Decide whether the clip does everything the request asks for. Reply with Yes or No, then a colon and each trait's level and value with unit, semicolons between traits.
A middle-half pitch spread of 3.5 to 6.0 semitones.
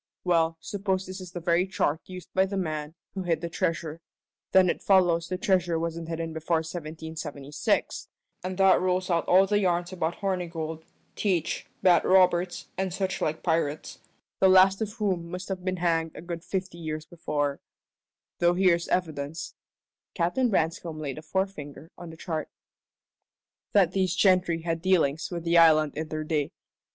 No: narrow, 2.5 semitones